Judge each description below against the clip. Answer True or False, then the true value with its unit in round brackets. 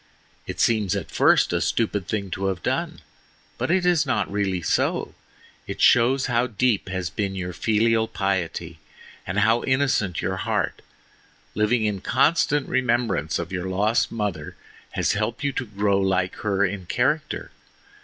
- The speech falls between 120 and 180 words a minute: True (155 wpm)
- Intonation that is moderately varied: True (4.4 semitones)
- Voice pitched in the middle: False (105 Hz)